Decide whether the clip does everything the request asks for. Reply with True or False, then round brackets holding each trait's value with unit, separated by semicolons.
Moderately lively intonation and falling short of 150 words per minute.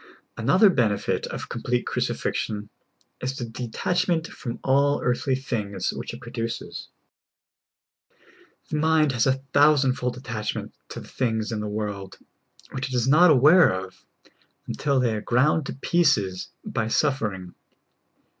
True (4.6 semitones; 140 wpm)